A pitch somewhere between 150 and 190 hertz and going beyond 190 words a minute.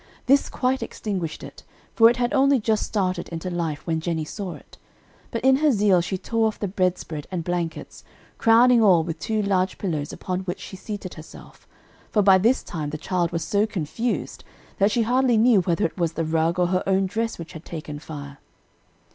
Yes: medium, 185 Hz; average, 200 wpm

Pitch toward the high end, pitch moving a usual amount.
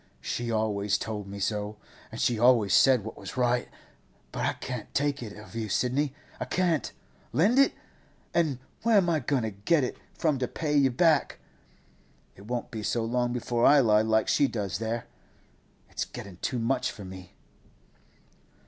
No: low, 120 Hz; average, 4.6 semitones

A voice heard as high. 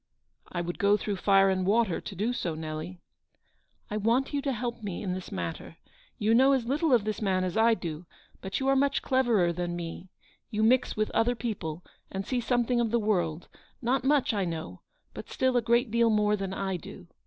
Yes: high, 210 Hz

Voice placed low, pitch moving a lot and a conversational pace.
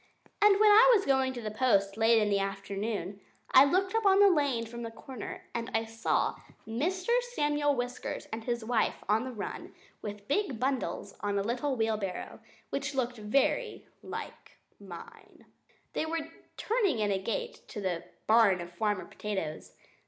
No: high, 235 Hz; wide, 5.9 semitones; average, 175 wpm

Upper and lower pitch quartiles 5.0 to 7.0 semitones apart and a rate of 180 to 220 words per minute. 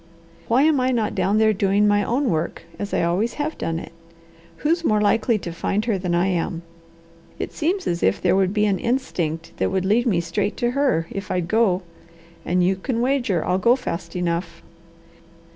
Yes: average, 5.3 semitones; average, 200 wpm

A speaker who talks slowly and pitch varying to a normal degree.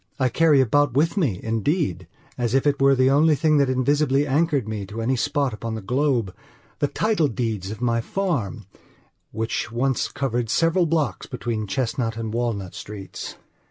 No: average, 160 wpm; average, 4.4 semitones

